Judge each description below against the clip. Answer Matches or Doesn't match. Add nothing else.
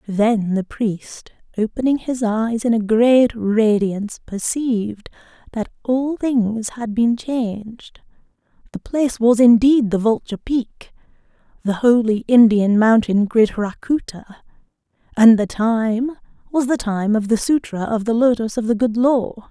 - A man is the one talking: Doesn't match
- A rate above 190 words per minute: Doesn't match